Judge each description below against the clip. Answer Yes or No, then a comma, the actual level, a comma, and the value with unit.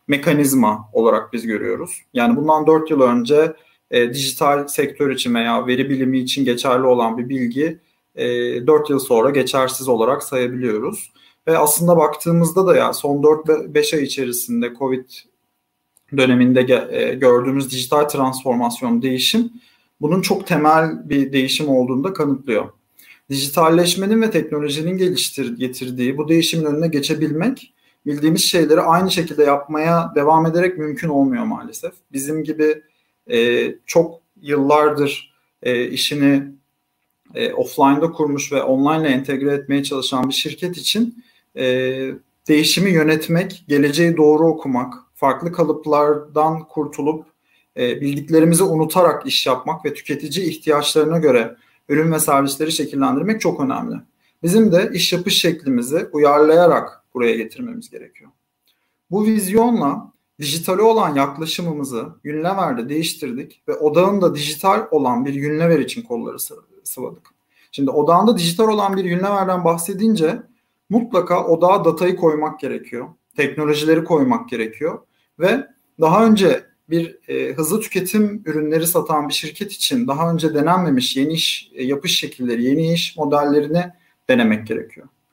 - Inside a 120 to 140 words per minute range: Yes, average, 125 wpm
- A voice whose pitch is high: No, medium, 155 Hz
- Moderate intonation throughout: Yes, average, 4.1 semitones